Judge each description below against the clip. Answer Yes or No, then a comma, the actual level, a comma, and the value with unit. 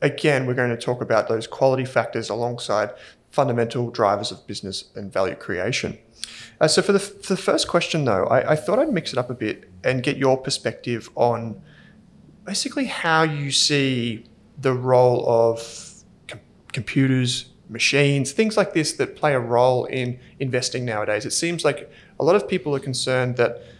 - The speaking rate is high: No, average, 180 wpm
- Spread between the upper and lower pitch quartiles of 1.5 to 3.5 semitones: No, average, 4.1 semitones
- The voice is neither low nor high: No, low, 130 Hz